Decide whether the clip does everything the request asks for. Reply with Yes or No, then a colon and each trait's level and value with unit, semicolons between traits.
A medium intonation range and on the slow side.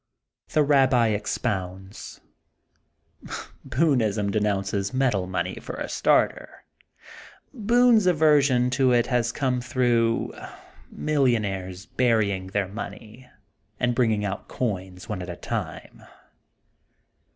Yes: average, 4.6 semitones; slow, 105 wpm